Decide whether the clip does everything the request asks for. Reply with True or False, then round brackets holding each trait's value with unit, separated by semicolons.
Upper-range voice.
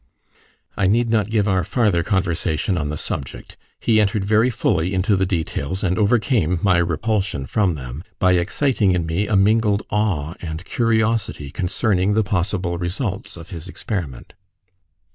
False (95 Hz)